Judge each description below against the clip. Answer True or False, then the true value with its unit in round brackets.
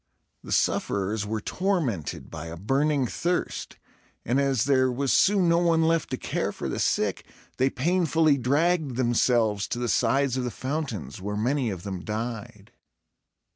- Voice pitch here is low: True (130 Hz)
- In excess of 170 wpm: False (160 wpm)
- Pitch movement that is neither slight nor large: False (5.9 semitones)